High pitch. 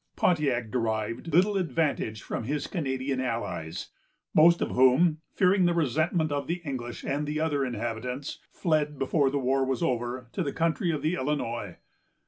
No: medium, 140 Hz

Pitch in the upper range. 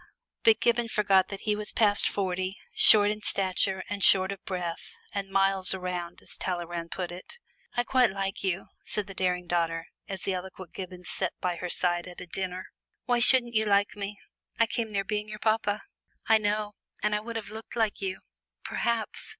Yes: high, 195 Hz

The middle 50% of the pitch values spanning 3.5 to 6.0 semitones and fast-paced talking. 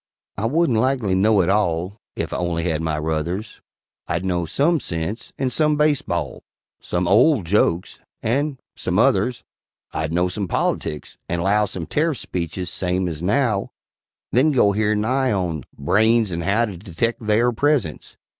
No: wide, 5.6 semitones; average, 165 wpm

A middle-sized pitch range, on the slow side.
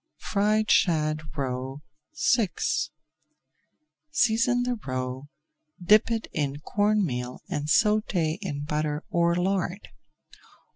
No: wide, 6.5 semitones; slow, 100 wpm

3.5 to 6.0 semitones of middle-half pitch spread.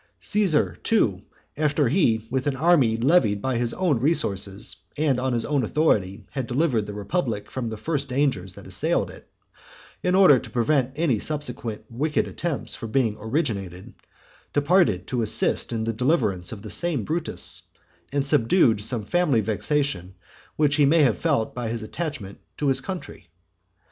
Yes: wide, 5.5 semitones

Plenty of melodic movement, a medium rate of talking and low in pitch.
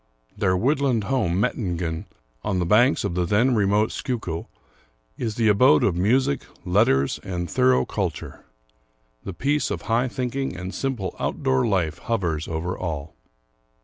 Yes: wide, 6.0 semitones; average, 150 wpm; low, 100 Hz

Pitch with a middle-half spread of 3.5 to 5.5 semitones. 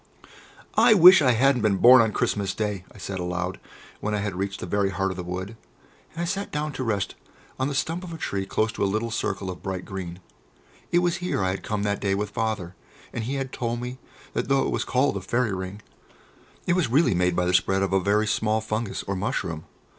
Yes: average, 5.1 semitones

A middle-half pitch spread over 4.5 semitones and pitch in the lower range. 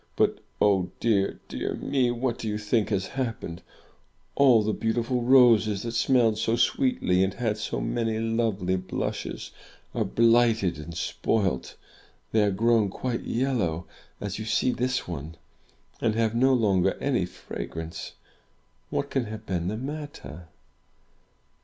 No: average, 3.8 semitones; low, 110 Hz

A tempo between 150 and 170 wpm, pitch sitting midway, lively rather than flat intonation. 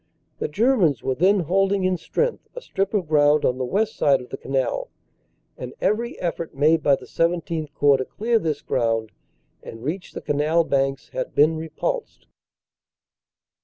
Yes: average, 165 wpm; medium, 160 Hz; wide, 5.7 semitones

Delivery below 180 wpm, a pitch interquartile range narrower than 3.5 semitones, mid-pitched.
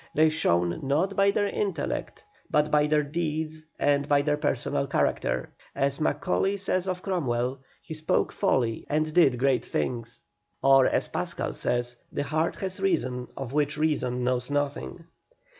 No: average, 155 wpm; average, 3.8 semitones; medium, 145 Hz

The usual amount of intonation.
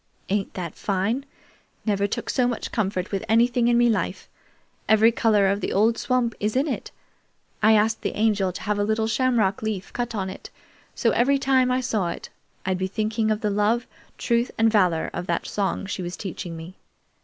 Yes: average, 3.3 semitones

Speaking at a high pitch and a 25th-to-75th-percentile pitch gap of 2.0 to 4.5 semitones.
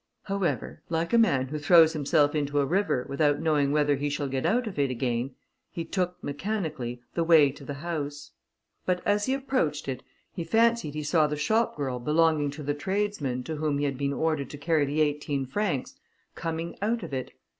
No: medium, 150 Hz; average, 3.3 semitones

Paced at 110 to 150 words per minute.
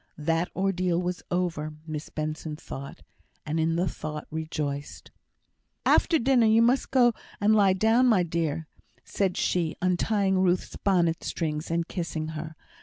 Yes: average, 145 wpm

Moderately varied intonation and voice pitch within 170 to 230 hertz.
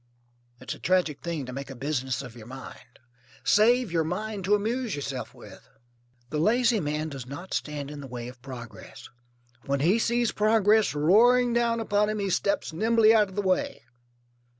No: wide, 7.7 semitones; medium, 185 Hz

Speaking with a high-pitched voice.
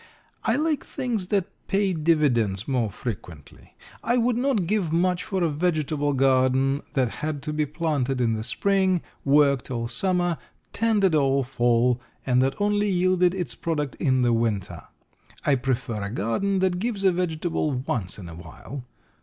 No: medium, 150 Hz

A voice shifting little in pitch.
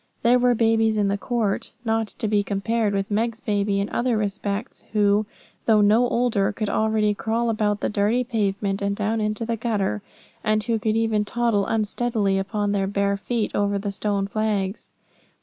Yes: narrow, 1.9 semitones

